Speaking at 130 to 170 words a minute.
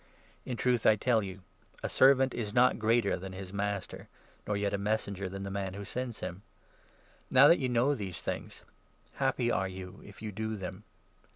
No: average, 200 wpm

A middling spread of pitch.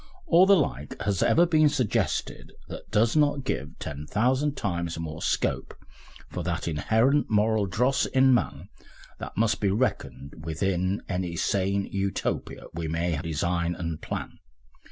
No: wide, 7.4 semitones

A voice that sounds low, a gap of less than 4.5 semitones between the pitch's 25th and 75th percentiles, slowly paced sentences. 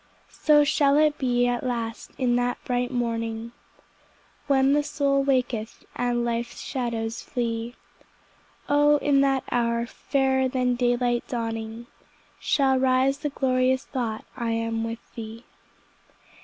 No: high, 245 Hz; narrow, 2.4 semitones; slow, 130 wpm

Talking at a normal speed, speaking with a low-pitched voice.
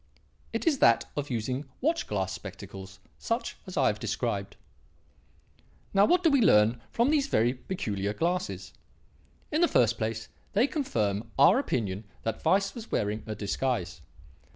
Yes: average, 150 wpm; low, 120 Hz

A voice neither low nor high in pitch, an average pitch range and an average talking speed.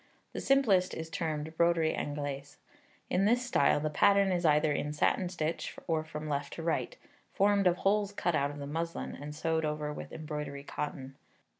Yes: medium, 160 Hz; average, 3.6 semitones; average, 180 wpm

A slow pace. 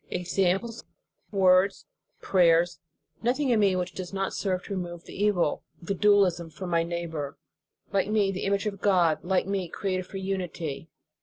No: average, 165 wpm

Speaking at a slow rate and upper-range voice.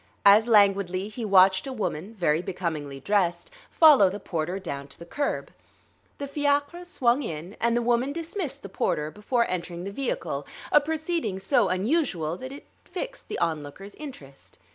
No: average, 165 wpm; high, 200 Hz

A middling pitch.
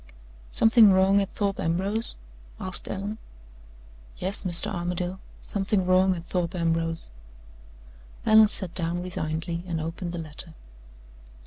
Yes: medium, 180 Hz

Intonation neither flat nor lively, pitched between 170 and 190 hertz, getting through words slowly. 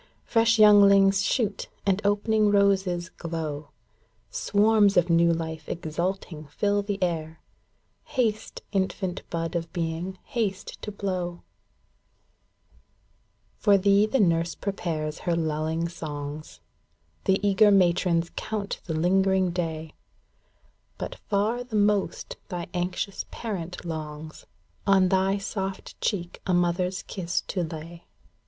Yes: average, 3.2 semitones; medium, 185 Hz; slow, 120 wpm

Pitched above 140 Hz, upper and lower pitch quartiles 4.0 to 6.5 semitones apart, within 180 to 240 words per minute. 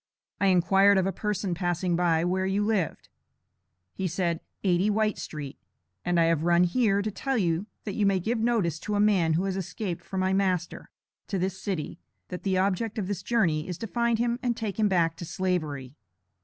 No: high, 190 Hz; average, 3.2 semitones; fast, 205 wpm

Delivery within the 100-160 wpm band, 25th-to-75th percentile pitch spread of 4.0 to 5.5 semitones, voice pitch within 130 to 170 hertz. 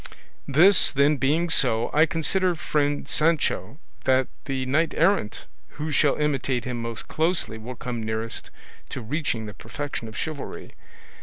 Yes: average, 145 wpm; average, 4.6 semitones; medium, 140 Hz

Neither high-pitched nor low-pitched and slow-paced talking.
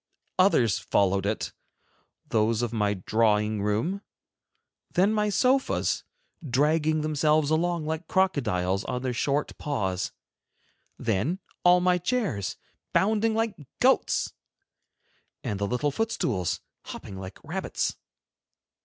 Yes: medium, 145 Hz; slow, 110 wpm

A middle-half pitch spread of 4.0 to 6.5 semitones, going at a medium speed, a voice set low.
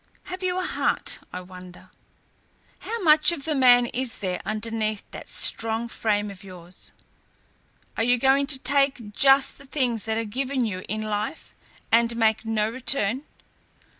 No: average, 4.3 semitones; average, 160 wpm; high, 230 Hz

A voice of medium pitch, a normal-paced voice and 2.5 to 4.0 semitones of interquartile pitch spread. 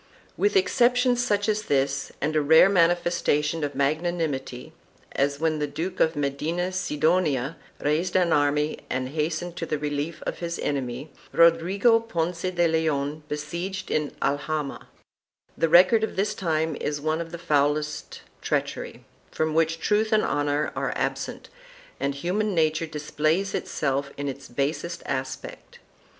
Yes: medium, 160 Hz; average, 145 wpm; average, 3.3 semitones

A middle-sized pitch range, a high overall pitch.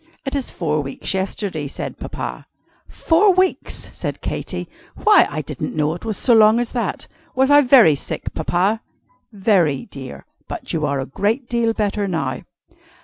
No: wide, 7.9 semitones; high, 205 Hz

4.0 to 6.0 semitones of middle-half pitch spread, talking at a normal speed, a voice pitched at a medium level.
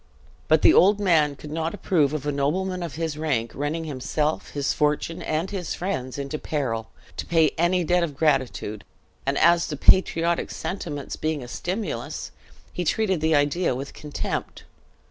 No: average, 3.3 semitones; average, 165 wpm; medium, 155 Hz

